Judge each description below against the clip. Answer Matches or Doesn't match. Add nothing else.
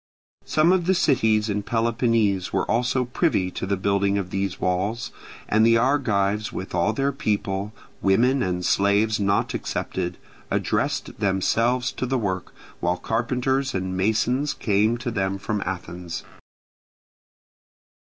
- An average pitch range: Matches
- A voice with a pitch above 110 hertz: Doesn't match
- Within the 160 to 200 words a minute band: Doesn't match